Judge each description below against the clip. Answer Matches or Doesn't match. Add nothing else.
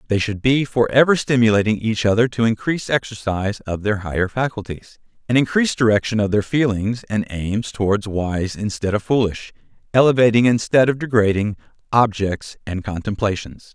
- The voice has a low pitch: Matches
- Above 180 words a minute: Doesn't match